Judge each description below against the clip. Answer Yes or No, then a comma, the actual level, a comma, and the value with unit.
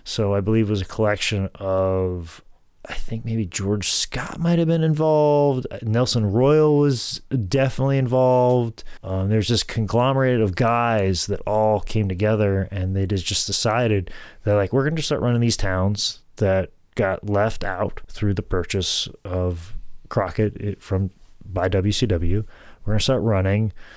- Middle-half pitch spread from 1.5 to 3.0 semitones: No, average, 4.0 semitones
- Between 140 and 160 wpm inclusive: Yes, average, 150 wpm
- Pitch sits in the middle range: No, low, 105 Hz